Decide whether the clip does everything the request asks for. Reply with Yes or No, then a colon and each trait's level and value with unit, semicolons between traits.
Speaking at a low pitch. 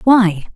No: high, 200 Hz